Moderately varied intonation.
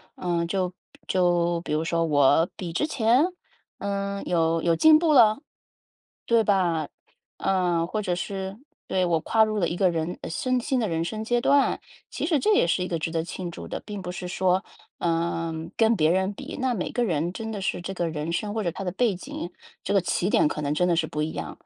Yes: average, 4.0 semitones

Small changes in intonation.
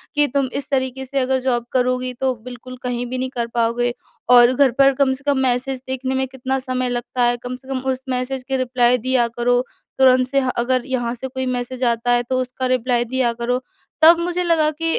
Yes: narrow, 1.3 semitones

